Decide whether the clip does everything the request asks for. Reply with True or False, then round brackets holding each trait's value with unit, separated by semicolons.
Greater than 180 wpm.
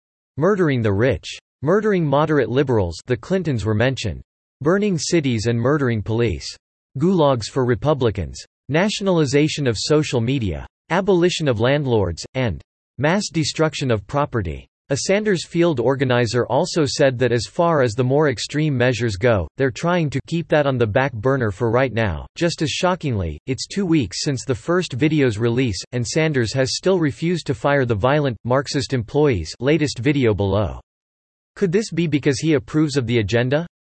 False (160 wpm)